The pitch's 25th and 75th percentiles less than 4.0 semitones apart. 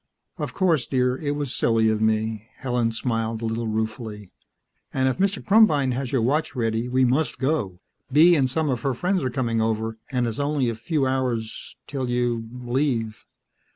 Yes: average, 3.6 semitones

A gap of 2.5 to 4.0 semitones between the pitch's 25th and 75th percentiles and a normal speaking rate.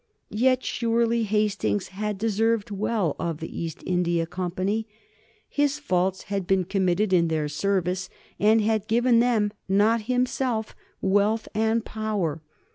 No: average, 3.5 semitones; slow, 130 wpm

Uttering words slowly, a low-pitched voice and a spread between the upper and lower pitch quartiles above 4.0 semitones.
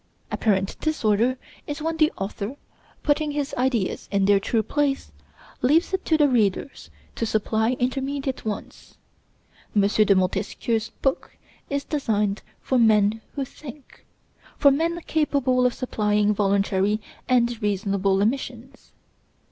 No: slow, 125 wpm; high, 235 Hz; average, 5.2 semitones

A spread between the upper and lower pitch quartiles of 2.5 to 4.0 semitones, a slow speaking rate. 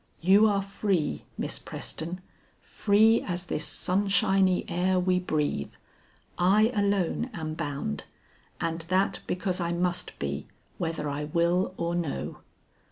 Yes: average, 3.0 semitones; slow, 125 wpm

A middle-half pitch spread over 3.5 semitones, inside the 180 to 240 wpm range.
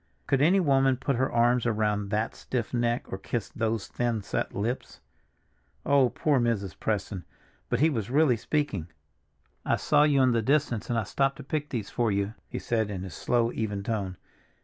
Yes: average, 4.2 semitones; average, 190 wpm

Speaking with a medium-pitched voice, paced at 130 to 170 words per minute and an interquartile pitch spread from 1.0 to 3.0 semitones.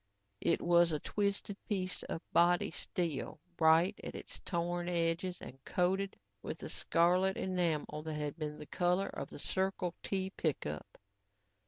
Yes: medium, 175 Hz; average, 150 wpm; average, 2.7 semitones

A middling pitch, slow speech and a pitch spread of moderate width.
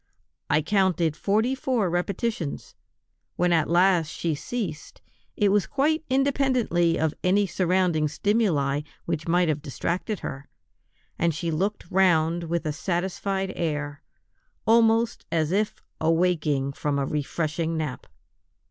Yes: medium, 175 Hz; slow, 125 wpm; average, 4.3 semitones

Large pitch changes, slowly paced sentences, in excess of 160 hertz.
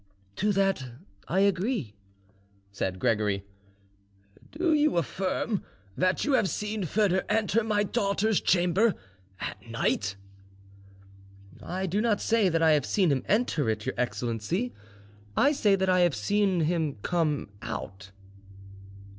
Yes: wide, 5.8 semitones; slow, 130 wpm; high, 190 Hz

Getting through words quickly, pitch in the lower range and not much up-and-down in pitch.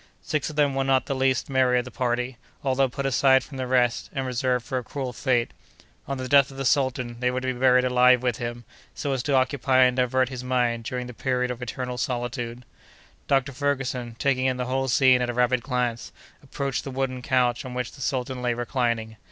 Yes: fast, 225 wpm; low, 125 Hz; narrow, 1.3 semitones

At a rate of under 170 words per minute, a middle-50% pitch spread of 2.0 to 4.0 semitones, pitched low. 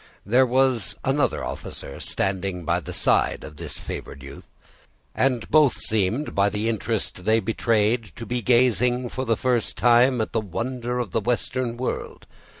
Yes: average, 160 wpm; average, 3.3 semitones; low, 115 Hz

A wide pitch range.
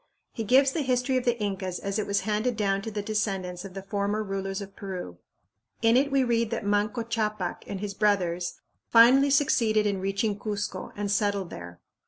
No: average, 2.8 semitones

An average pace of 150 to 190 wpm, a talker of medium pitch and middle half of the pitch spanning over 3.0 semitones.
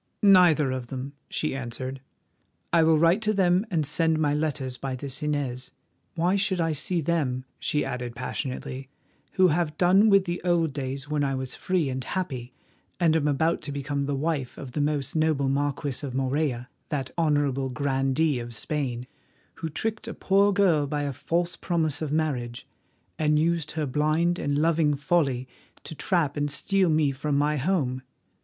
Yes: average, 175 wpm; medium, 150 Hz; average, 3.7 semitones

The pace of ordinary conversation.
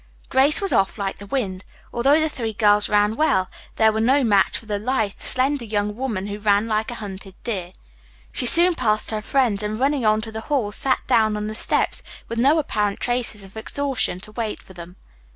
No: fast, 210 wpm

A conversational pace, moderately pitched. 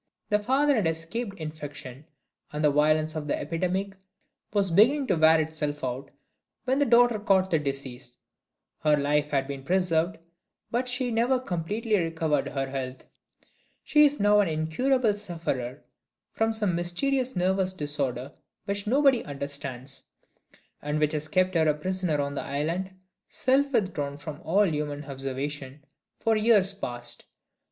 Yes: average, 145 wpm; medium, 165 Hz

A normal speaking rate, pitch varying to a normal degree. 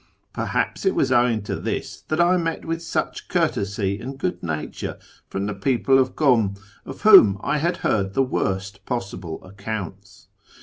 No: average, 165 wpm; wide, 7.4 semitones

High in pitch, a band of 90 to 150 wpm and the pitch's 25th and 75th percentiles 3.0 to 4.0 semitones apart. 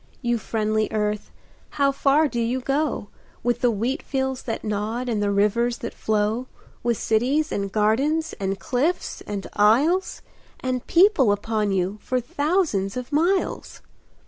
No: high, 240 Hz; average, 145 wpm; average, 4.6 semitones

